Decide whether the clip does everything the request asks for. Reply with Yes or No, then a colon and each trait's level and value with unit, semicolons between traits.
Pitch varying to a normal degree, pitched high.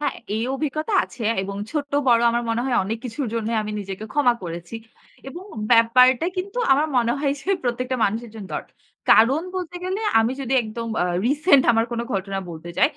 Yes: average, 4.3 semitones; high, 240 Hz